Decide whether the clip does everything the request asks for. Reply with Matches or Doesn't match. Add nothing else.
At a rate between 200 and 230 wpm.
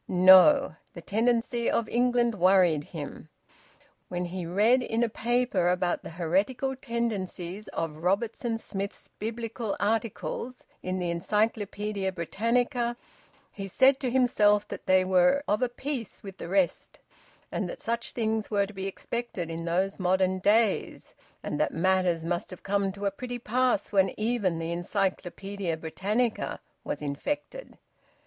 Doesn't match